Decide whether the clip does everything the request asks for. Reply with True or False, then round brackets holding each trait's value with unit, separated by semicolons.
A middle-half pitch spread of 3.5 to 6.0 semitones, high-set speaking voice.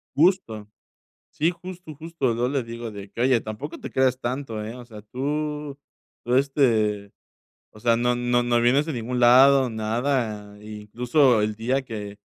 False (4.0 semitones; 120 Hz)